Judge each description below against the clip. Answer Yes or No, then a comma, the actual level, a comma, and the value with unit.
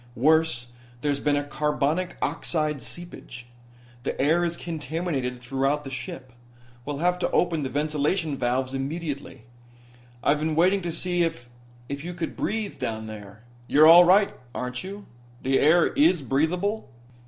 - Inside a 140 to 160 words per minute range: Yes, average, 150 wpm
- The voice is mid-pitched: Yes, medium, 150 Hz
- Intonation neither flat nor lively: Yes, average, 4.4 semitones